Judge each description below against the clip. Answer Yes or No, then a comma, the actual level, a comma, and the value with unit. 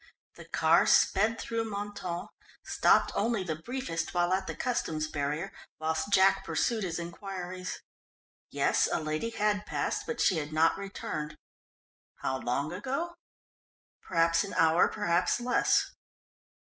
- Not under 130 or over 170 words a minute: Yes, slow, 135 wpm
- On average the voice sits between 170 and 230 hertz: Yes, medium, 185 Hz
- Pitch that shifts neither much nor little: Yes, average, 4.5 semitones